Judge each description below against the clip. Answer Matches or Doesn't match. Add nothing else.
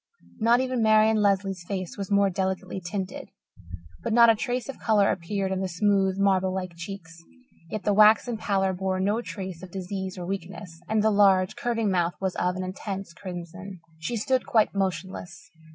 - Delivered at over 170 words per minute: Matches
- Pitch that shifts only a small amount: Matches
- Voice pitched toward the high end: Matches